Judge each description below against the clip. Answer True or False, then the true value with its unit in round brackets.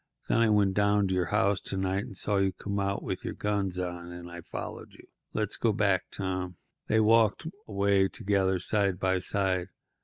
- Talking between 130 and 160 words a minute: False (195 wpm)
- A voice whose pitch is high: False (95 Hz)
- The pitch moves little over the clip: True (1.8 semitones)